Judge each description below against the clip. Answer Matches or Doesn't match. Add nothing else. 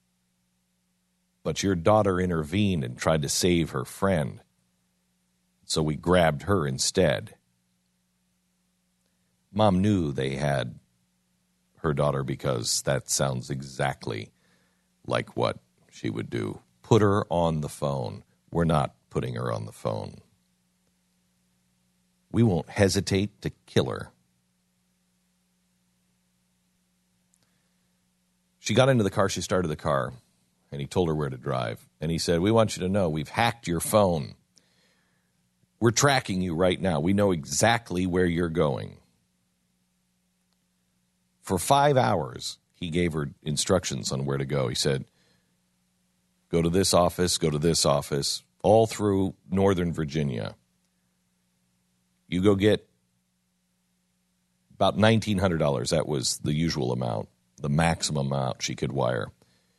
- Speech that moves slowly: Matches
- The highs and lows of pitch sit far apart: Matches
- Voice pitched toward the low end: Matches